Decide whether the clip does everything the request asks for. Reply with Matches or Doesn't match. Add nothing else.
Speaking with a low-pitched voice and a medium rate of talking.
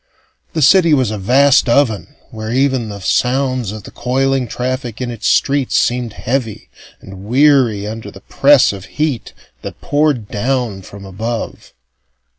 Matches